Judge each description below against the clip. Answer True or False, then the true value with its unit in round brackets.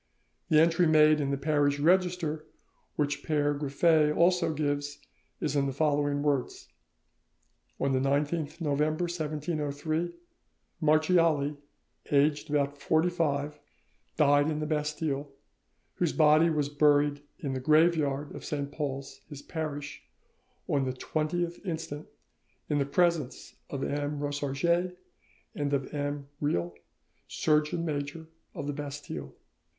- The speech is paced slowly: True (125 wpm)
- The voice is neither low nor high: True (150 Hz)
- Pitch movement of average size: False (1.7 semitones)